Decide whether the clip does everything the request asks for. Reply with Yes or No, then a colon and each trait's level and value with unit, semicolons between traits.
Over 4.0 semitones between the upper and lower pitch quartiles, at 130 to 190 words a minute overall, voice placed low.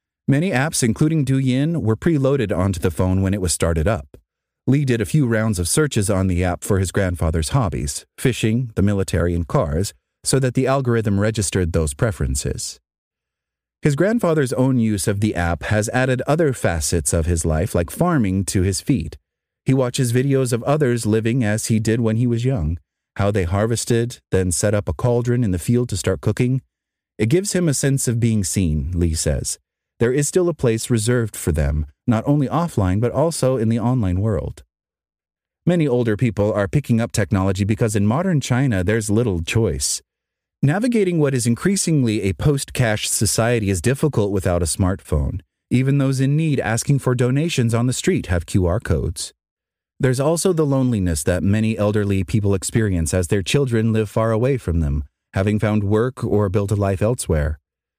Yes: wide, 5.5 semitones; average, 180 wpm; low, 110 Hz